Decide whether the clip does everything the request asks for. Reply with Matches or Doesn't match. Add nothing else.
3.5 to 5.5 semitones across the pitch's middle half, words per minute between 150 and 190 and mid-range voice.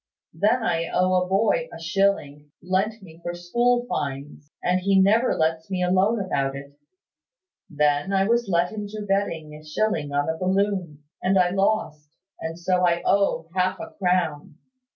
Matches